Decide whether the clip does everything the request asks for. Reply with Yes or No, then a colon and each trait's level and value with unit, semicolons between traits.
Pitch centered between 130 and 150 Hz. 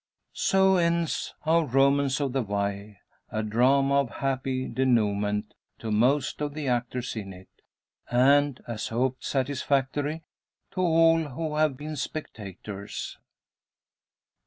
Yes: low, 135 Hz